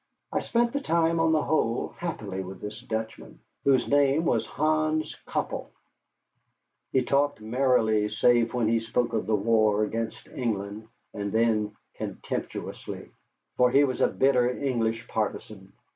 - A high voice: No, low, 115 Hz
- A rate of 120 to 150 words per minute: Yes, average, 145 wpm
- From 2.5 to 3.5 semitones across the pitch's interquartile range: No, average, 4.3 semitones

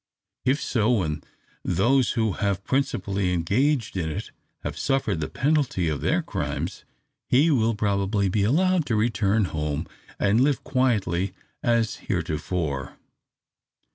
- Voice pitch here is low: Yes, low, 105 Hz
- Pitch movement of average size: No, wide, 5.9 semitones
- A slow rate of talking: Yes, slow, 130 wpm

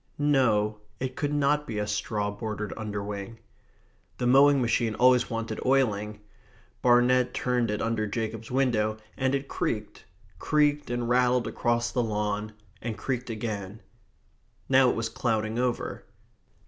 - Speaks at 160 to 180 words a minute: No, slow, 135 wpm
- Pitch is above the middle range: No, low, 115 Hz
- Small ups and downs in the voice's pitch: No, average, 3.0 semitones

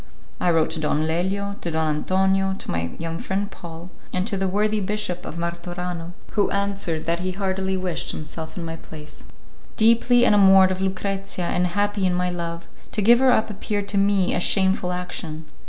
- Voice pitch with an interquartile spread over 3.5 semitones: No, average, 2.9 semitones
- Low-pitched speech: No, medium, 185 Hz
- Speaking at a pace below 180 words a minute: No, average, 190 wpm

